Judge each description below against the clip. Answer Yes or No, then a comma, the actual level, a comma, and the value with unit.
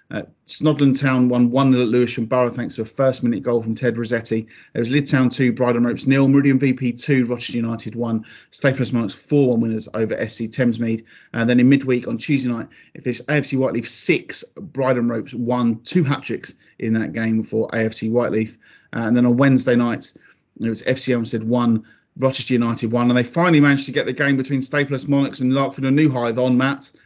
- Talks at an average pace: No, fast, 210 wpm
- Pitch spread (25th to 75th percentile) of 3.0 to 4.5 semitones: No, narrow, 2.6 semitones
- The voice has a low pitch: Yes, low, 125 Hz